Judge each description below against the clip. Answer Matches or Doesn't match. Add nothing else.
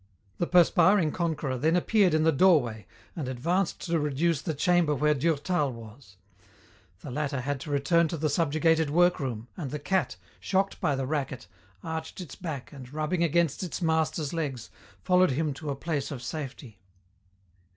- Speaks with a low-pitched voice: Doesn't match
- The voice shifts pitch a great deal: Doesn't match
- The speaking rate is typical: Matches